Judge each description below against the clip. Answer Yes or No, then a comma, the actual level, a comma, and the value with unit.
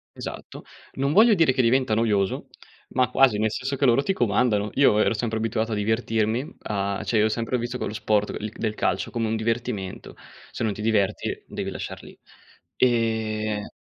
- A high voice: No, low, 110 Hz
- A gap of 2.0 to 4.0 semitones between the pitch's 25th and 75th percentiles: Yes, average, 2.7 semitones